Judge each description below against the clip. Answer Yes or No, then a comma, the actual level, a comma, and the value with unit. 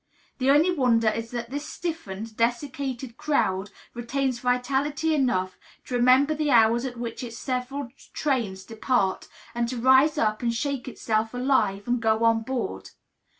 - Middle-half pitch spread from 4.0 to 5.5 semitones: No, average, 3.1 semitones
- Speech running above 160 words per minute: No, average, 150 wpm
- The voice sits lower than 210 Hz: No, high, 245 Hz